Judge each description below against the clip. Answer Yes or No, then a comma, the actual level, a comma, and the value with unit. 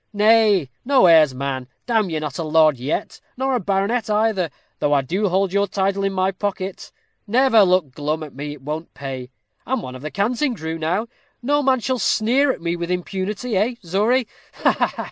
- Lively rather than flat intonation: Yes, wide, 6.1 semitones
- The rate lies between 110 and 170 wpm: No, average, 200 wpm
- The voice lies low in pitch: No, high, 190 Hz